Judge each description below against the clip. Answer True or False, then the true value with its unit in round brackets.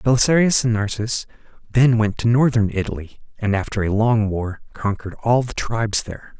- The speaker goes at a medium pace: True (170 wpm)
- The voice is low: True (110 Hz)